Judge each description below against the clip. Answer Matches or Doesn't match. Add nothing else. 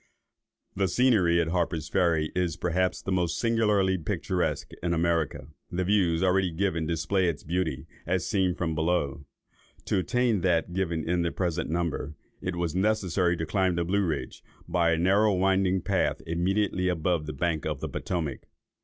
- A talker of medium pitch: Doesn't match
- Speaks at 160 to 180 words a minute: Matches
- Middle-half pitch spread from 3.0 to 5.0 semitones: Doesn't match